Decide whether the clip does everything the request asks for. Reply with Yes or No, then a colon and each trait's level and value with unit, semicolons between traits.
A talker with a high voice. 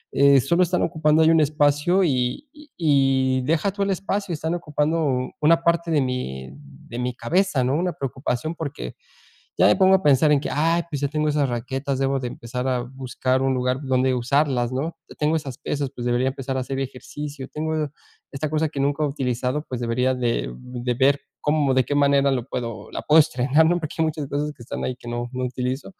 No: medium, 140 Hz